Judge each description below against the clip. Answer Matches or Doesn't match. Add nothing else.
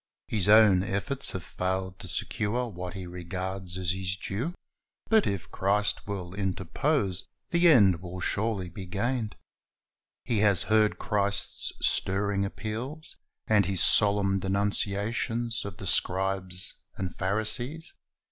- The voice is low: Matches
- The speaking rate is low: Matches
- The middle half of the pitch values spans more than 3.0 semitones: Doesn't match